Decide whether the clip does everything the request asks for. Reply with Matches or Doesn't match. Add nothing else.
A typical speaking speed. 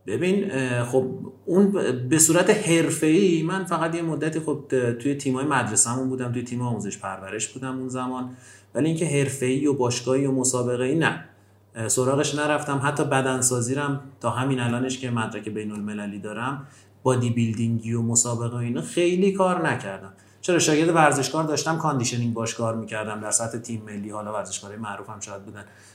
Doesn't match